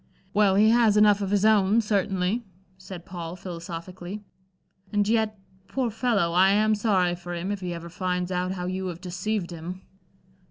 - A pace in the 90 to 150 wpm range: No, average, 170 wpm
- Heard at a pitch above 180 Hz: Yes, high, 190 Hz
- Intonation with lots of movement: No, average, 2.8 semitones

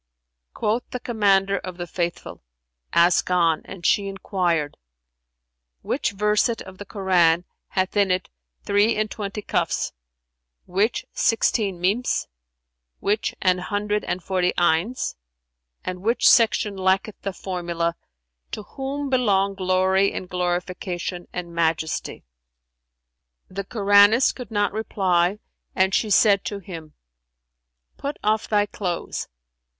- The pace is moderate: No, slow, 120 wpm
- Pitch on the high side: Yes, high, 195 Hz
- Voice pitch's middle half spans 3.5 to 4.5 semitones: No, average, 2.7 semitones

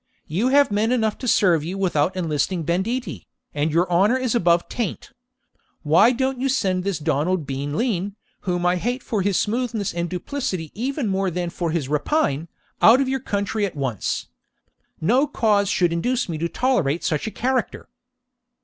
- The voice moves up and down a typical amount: No, wide, 6.1 semitones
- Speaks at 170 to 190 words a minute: Yes, average, 175 wpm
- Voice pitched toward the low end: No, high, 190 Hz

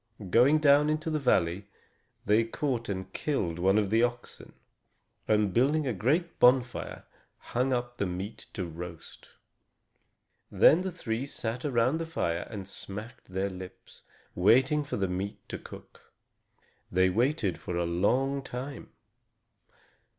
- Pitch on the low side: Yes, low, 115 Hz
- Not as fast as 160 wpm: Yes, average, 140 wpm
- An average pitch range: No, wide, 6.3 semitones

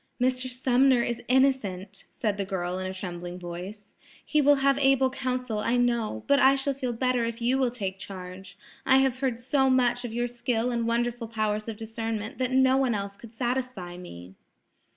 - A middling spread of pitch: Yes, average, 4.2 semitones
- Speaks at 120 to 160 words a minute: No, average, 195 wpm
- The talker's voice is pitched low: No, high, 240 Hz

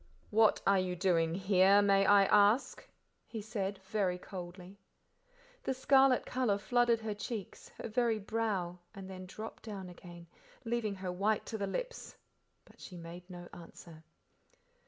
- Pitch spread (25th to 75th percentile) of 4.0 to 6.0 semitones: No, average, 3.3 semitones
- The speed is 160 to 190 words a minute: No, average, 150 wpm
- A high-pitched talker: Yes, high, 200 Hz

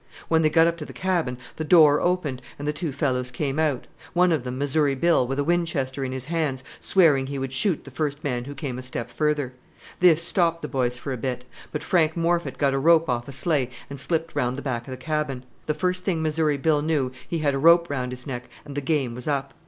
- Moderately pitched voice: Yes, medium, 145 Hz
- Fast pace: Yes, fast, 245 wpm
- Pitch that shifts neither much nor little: Yes, average, 3.7 semitones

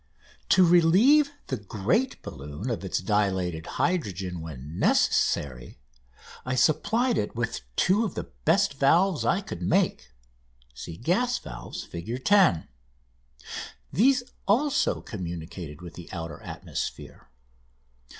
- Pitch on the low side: Yes, low, 115 Hz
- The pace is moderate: No, slow, 110 wpm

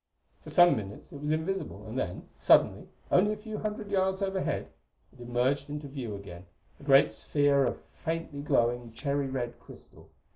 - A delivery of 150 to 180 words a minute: Yes, average, 170 wpm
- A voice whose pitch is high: No, medium, 140 Hz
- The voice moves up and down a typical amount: No, wide, 6.4 semitones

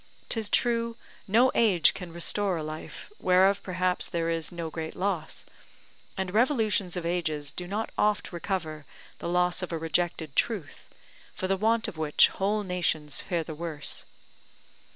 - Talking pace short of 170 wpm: Yes, average, 155 wpm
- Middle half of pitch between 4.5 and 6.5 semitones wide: No, average, 3.8 semitones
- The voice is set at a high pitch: No, medium, 180 Hz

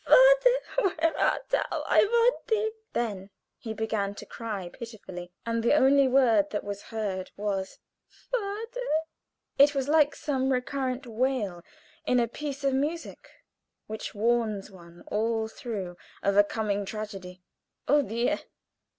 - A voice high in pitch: Yes, high, 235 Hz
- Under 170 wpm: Yes, average, 140 wpm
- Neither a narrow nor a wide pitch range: No, wide, 6.0 semitones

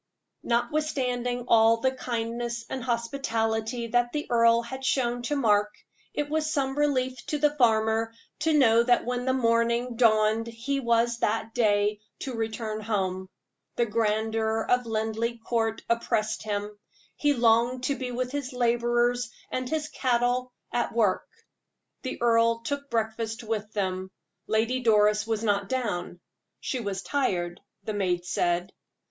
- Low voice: No, high, 230 Hz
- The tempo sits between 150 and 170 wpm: No, average, 140 wpm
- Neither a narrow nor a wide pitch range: No, narrow, 2.3 semitones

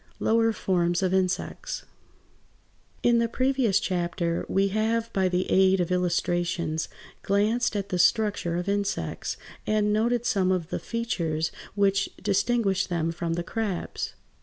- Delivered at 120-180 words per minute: Yes, slow, 135 wpm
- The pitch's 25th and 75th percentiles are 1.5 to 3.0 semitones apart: No, average, 3.7 semitones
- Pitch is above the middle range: Yes, high, 195 Hz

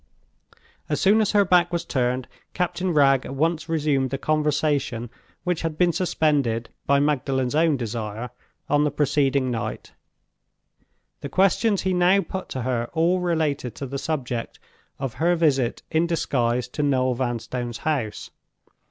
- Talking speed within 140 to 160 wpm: Yes, average, 150 wpm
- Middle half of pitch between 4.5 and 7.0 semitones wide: Yes, average, 4.8 semitones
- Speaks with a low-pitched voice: No, medium, 145 Hz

